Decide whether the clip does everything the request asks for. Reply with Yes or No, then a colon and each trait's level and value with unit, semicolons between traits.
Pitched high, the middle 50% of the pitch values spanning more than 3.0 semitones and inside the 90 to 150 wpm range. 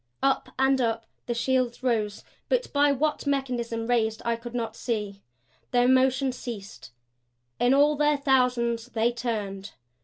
No: high, 245 Hz; average, 2.7 semitones; average, 145 wpm